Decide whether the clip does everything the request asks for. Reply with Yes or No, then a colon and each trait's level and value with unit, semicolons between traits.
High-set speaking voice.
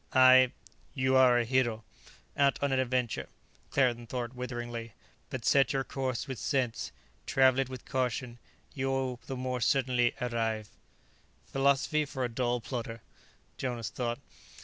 No: low, 125 Hz